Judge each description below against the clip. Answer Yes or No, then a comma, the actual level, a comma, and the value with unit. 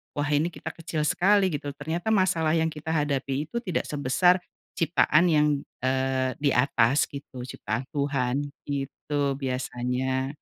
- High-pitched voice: No, medium, 145 Hz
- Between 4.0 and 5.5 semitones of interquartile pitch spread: No, average, 3.3 semitones